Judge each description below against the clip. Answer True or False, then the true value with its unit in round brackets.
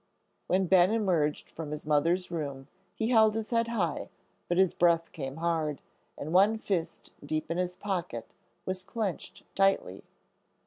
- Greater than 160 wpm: False (150 wpm)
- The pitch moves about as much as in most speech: True (3.8 semitones)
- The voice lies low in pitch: False (175 Hz)